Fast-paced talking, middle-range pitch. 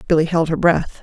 Yes: fast, 235 wpm; medium, 165 Hz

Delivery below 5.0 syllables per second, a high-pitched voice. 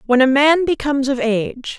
No: 5.5 syllables/s; very high, 270 Hz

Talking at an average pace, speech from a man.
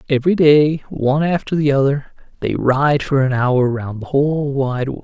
Yes: average, 190 wpm; male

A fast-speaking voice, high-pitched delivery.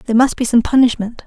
Yes: fast, 235 wpm; high, 240 Hz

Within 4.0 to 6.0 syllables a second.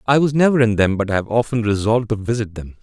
No: 6.8 syllables/s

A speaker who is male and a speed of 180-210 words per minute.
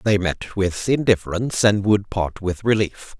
No: male; average, 170 wpm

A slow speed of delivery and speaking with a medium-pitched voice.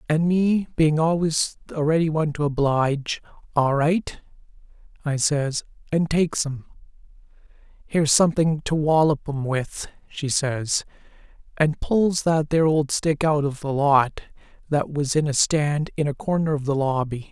No: average, 155 wpm; medium, 150 Hz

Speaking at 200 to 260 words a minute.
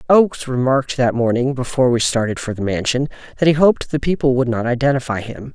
Yes: fast, 205 wpm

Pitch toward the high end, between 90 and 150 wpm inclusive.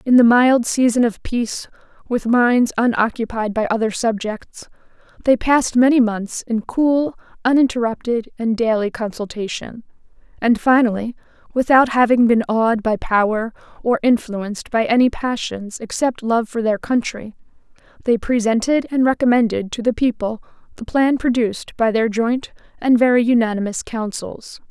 Yes: high, 235 Hz; average, 140 wpm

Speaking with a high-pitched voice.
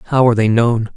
No: low, 115 Hz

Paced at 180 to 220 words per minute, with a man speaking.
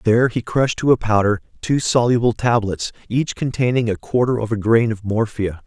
Yes: average, 190 wpm; male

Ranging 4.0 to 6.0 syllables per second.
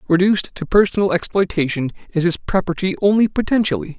No: 6.2 syllables/s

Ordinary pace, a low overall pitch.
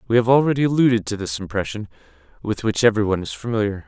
Yes: average, 185 wpm; low, 110 Hz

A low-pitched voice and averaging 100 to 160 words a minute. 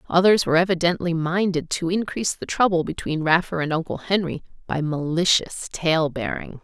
No: medium, 170 Hz; average, 155 wpm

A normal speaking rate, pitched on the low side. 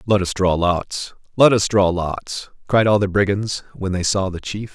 No: fast, 215 wpm; low, 100 Hz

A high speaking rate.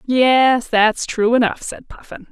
No: average, 155 wpm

